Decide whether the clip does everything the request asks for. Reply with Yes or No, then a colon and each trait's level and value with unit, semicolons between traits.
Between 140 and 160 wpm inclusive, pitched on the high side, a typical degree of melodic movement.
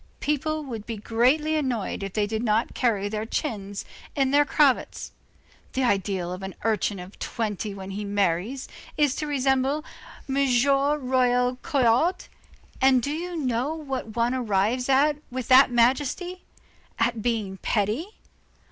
Yes: average, 145 wpm; high, 245 Hz; average, 4.8 semitones